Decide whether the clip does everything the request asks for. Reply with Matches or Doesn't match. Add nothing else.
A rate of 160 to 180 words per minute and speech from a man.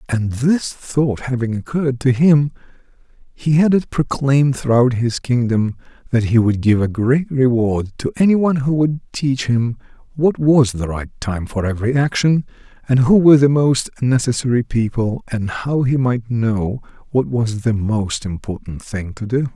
Matches